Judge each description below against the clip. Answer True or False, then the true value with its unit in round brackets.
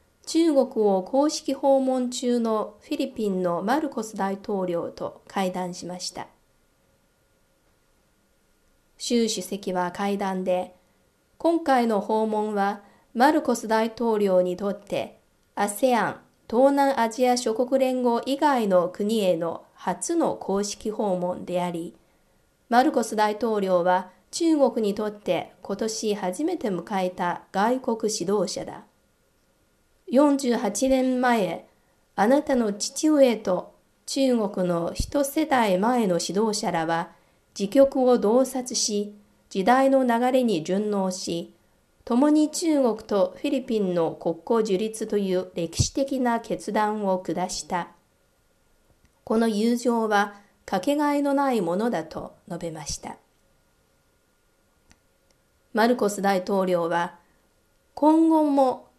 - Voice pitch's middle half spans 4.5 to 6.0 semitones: True (5.6 semitones)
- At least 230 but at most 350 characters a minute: False (210 characters per minute)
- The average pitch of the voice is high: True (220 Hz)